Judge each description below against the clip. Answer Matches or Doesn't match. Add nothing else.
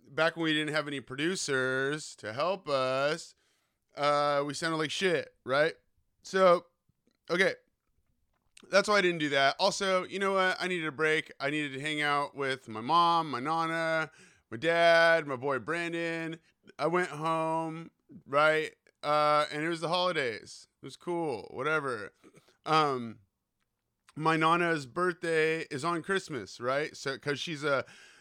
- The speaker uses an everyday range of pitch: Matches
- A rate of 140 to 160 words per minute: Matches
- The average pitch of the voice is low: Doesn't match